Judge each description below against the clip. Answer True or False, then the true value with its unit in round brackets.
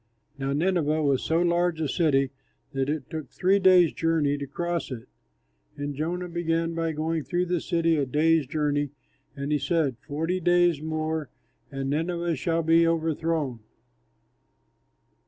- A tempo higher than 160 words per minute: False (150 wpm)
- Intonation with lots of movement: False (2.8 semitones)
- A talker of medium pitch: True (160 Hz)